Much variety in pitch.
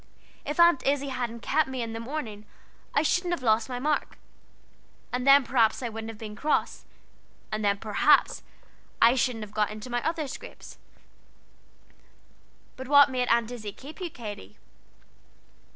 No: average, 4.3 semitones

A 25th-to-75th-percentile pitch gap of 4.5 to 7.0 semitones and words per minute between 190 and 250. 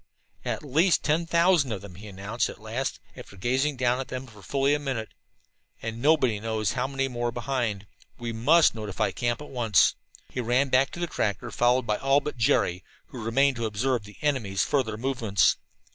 No: average, 3.8 semitones; average, 195 wpm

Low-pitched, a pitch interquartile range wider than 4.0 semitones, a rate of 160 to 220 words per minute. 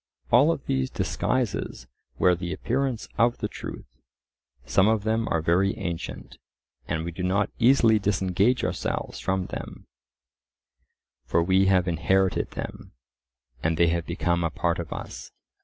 No: very low, 95 Hz; average, 4.4 semitones; average, 145 wpm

